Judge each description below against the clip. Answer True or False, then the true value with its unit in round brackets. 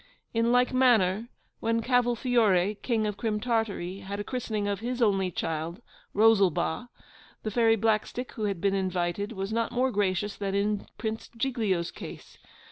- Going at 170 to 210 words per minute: False (155 wpm)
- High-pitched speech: True (215 Hz)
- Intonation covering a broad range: False (3.0 semitones)